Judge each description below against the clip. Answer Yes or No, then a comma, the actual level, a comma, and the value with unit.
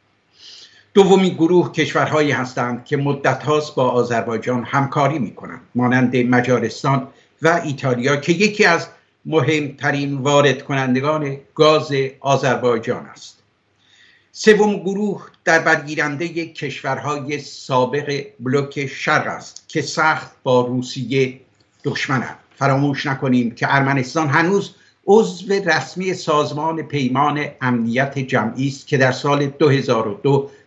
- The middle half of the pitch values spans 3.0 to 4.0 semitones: Yes, average, 3.3 semitones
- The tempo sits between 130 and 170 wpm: No, average, 110 wpm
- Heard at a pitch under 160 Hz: Yes, medium, 140 Hz